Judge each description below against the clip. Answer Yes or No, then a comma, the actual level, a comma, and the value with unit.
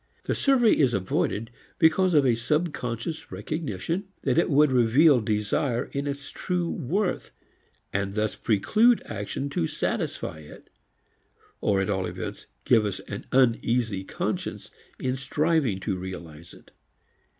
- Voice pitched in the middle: No, low, 125 Hz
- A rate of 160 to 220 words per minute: No, slow, 135 wpm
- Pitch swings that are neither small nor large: No, wide, 7.2 semitones